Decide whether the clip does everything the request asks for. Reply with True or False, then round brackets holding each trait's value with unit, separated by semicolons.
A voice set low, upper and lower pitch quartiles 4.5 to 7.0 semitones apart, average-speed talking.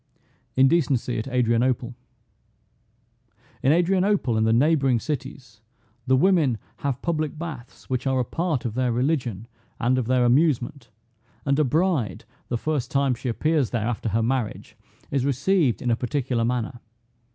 False (130 Hz; 3.9 semitones; 150 wpm)